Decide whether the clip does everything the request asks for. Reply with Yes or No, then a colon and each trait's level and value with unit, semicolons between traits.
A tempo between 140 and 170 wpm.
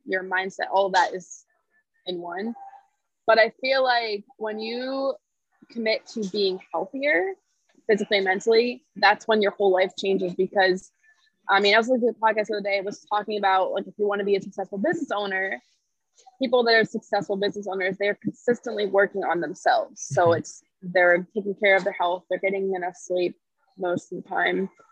No: average, 195 wpm